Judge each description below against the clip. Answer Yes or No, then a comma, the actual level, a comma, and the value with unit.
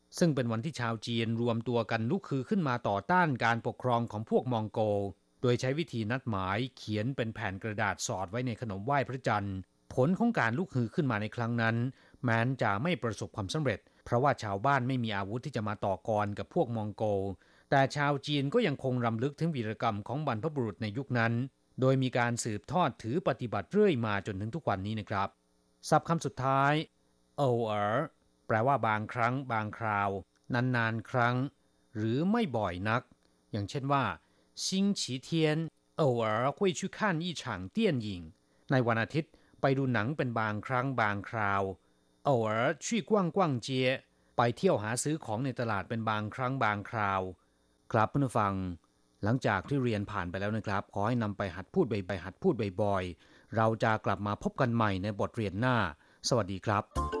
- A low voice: Yes, low, 115 Hz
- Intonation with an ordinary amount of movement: Yes, average, 4.7 semitones